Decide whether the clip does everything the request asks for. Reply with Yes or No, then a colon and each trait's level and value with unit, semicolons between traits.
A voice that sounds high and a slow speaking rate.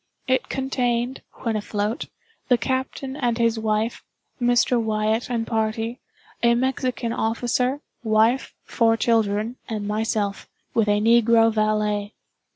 Yes: high, 230 Hz; slow, 120 wpm